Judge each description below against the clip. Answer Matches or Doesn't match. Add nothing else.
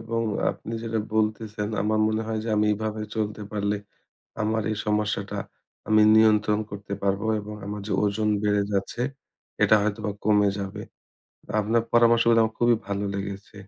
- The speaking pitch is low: Matches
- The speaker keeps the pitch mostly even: Matches